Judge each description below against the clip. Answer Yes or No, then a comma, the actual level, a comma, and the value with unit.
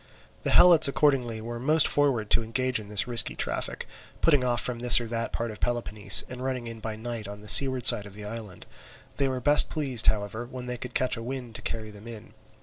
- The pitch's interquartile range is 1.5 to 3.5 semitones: Yes, average, 2.7 semitones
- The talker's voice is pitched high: No, low, 120 Hz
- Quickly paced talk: Yes, fast, 230 wpm